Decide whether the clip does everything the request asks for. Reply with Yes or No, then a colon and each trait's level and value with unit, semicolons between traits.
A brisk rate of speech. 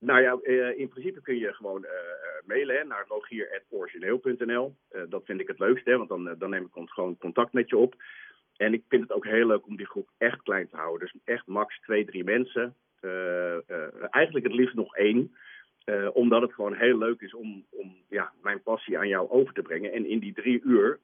Yes: fast, 210 wpm